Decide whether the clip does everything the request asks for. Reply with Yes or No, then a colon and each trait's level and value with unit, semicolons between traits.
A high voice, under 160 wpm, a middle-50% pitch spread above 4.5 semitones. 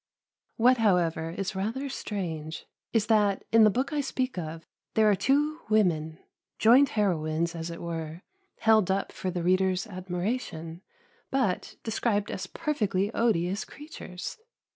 Yes: high, 195 Hz; average, 140 wpm; average, 4.9 semitones